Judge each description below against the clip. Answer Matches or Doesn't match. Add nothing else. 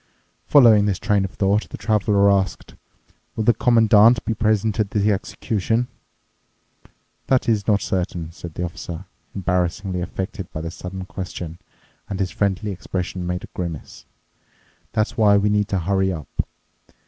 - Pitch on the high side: Doesn't match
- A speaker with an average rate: Matches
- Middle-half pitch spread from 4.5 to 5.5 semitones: Doesn't match